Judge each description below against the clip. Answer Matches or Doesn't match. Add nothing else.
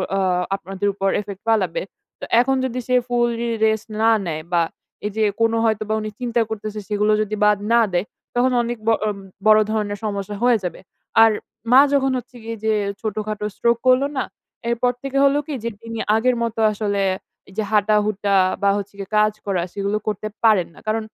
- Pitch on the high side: Matches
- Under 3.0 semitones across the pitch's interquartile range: Matches